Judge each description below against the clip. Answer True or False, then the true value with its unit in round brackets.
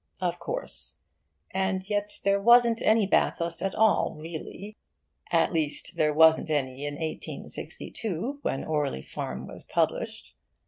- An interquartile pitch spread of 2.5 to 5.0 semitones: False (5.4 semitones)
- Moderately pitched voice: True (170 Hz)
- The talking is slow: True (130 wpm)